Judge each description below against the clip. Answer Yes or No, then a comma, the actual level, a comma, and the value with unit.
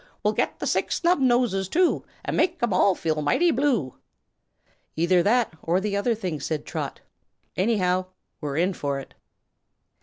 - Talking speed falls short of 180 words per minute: Yes, average, 150 wpm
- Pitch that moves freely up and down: Yes, wide, 6.6 semitones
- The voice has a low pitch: No, high, 190 Hz